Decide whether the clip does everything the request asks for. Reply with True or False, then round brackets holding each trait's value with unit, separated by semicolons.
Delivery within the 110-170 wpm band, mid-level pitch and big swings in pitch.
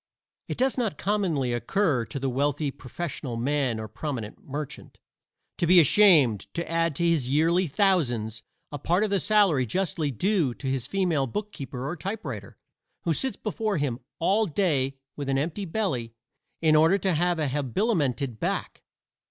True (160 wpm; 155 Hz; 6.1 semitones)